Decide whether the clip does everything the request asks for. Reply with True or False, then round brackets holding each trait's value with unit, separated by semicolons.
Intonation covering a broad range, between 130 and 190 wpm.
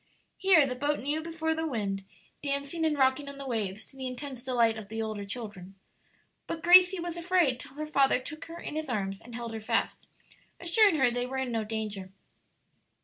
False (5.9 semitones; 205 wpm)